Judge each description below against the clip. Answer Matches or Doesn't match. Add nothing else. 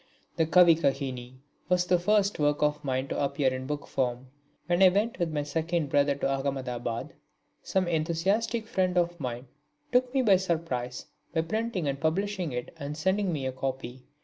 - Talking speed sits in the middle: Matches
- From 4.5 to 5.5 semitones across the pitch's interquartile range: Matches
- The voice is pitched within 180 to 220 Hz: Doesn't match